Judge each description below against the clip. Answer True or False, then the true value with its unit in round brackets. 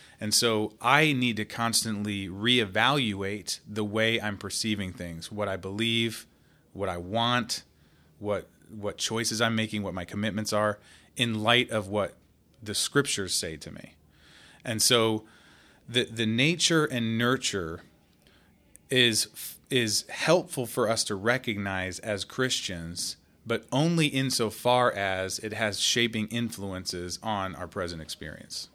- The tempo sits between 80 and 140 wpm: True (135 wpm)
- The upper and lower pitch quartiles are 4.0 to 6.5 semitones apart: False (3.2 semitones)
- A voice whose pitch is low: True (110 Hz)